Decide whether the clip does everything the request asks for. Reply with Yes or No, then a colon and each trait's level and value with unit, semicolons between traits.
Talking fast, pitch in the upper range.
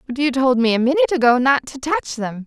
Yes: fast, 270 wpm; very high, 265 Hz